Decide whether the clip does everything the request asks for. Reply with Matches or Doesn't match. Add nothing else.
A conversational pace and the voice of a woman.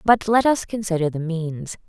Matches